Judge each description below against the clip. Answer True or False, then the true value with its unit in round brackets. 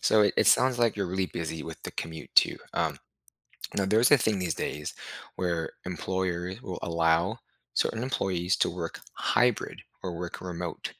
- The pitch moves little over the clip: False (3.4 semitones)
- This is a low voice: True (90 Hz)